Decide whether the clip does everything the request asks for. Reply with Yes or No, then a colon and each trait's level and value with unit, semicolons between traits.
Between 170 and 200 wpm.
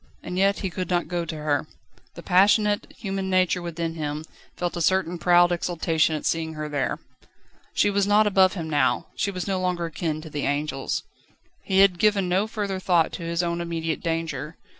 Yes: average, 195 wpm